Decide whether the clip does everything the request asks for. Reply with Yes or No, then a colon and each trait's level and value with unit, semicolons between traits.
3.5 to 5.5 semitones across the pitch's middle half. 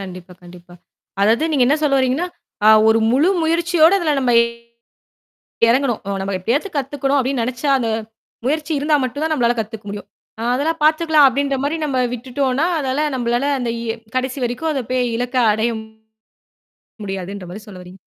Yes: average, 4.6 semitones